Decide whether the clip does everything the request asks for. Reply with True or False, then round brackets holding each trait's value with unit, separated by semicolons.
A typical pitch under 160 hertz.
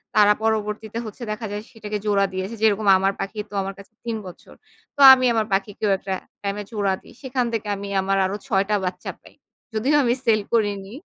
False (210 Hz)